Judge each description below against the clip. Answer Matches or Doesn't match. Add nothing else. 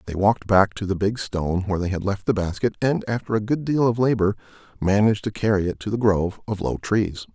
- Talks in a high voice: Doesn't match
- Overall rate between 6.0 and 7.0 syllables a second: Matches